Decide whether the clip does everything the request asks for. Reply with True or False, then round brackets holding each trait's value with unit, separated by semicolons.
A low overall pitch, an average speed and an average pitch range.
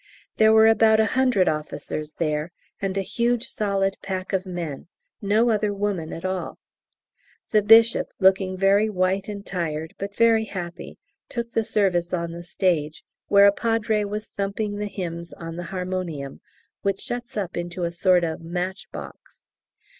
False (195 Hz; 160 wpm; 3.5 semitones)